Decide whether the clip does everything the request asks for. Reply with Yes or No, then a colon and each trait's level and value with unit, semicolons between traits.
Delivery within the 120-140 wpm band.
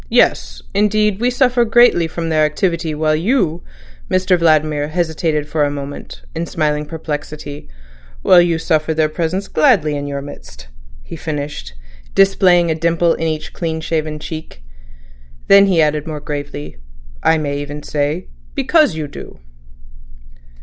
Yes: slow, 135 wpm